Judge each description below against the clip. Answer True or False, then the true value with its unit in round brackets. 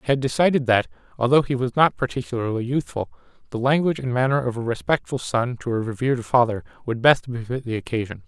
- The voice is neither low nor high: False (125 Hz)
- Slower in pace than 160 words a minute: False (195 wpm)